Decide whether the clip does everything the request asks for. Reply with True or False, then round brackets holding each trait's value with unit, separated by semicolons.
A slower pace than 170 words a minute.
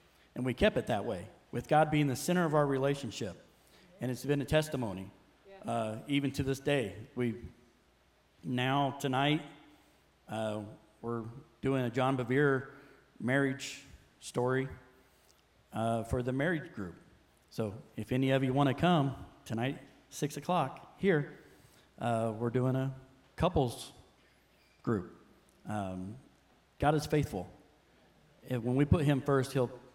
True (140 wpm)